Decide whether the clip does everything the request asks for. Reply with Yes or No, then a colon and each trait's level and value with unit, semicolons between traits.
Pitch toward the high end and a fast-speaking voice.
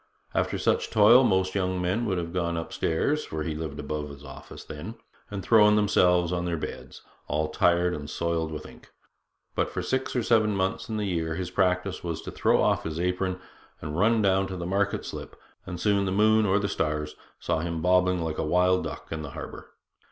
No: very low, 90 Hz; fast, 210 wpm